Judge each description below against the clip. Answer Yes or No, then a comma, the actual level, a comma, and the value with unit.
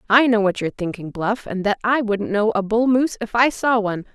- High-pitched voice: Yes, high, 215 Hz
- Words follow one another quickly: Yes, fast, 260 wpm